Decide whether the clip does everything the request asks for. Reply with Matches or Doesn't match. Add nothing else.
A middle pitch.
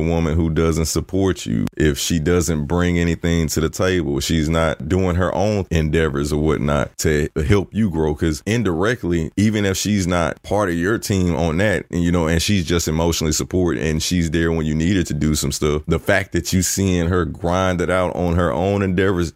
Doesn't match